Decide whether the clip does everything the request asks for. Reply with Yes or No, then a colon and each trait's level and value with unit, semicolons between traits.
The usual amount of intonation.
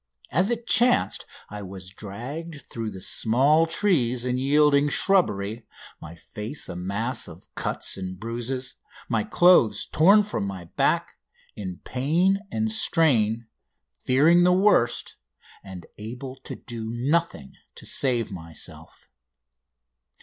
No: wide, 7.7 semitones